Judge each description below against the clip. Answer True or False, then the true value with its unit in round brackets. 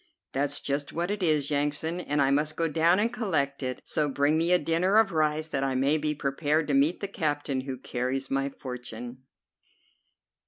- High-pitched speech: False (145 Hz)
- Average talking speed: True (195 wpm)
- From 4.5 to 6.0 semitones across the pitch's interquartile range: False (3.0 semitones)